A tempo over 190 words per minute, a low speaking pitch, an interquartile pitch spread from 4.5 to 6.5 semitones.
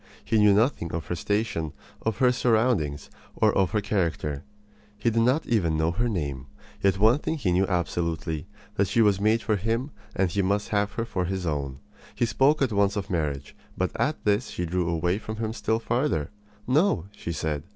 Yes: average, 200 wpm; low, 100 Hz; average, 5.1 semitones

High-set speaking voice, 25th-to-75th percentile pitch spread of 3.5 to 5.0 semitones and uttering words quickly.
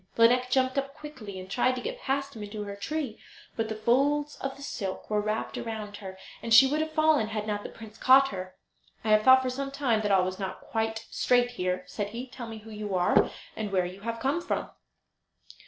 Yes: high, 225 Hz; average, 4.3 semitones; fast, 230 wpm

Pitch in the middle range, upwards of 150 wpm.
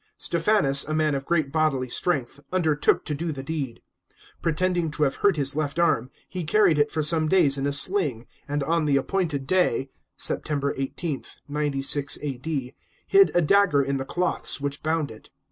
Yes: medium, 150 Hz; average, 180 wpm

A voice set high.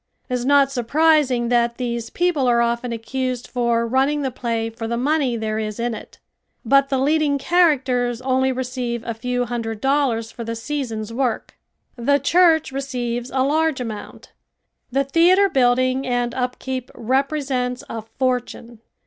Yes: very high, 250 Hz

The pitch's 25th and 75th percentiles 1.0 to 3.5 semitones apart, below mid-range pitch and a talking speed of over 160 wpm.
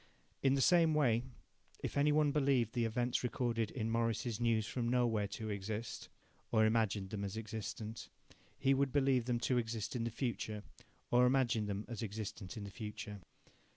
Yes: narrow, 2.6 semitones; low, 115 Hz; average, 175 wpm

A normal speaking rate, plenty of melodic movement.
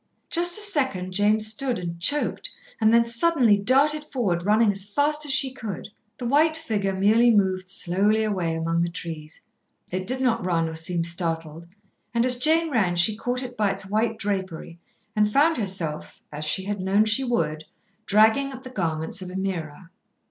Yes: average, 180 wpm; wide, 5.8 semitones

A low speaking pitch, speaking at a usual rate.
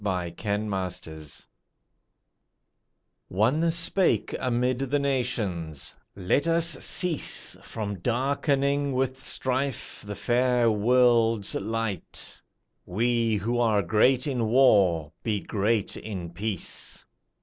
No: low, 115 Hz; slow, 95 wpm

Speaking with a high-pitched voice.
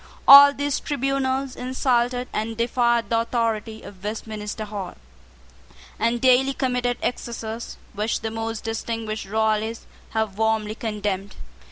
Yes: high, 225 Hz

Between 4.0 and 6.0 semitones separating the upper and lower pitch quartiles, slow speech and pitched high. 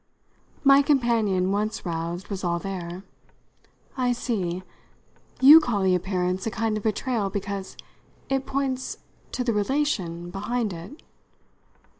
Yes: average, 5.1 semitones; slow, 125 wpm; high, 205 Hz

